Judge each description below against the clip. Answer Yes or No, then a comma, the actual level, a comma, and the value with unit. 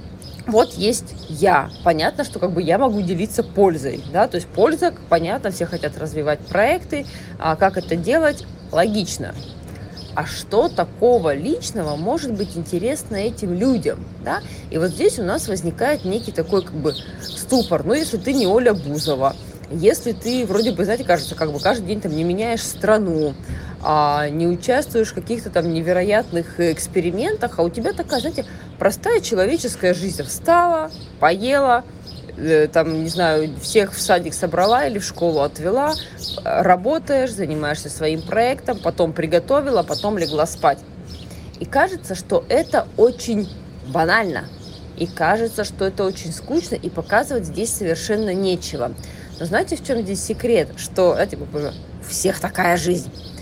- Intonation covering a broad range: Yes, wide, 6.2 semitones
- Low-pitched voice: No, high, 190 Hz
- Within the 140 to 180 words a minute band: Yes, average, 150 wpm